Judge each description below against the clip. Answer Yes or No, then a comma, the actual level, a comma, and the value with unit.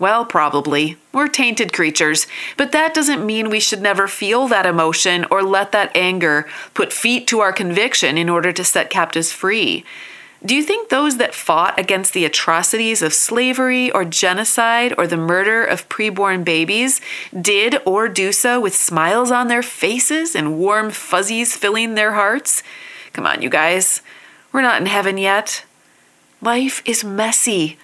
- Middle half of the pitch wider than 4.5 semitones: Yes, average, 4.9 semitones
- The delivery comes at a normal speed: Yes, average, 165 wpm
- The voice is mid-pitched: No, high, 210 Hz